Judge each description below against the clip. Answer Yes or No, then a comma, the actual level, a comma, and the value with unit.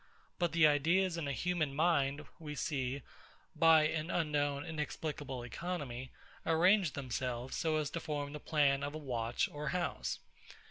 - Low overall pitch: No, medium, 150 Hz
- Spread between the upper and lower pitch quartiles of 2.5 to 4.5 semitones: Yes, average, 2.9 semitones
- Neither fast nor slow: Yes, average, 150 wpm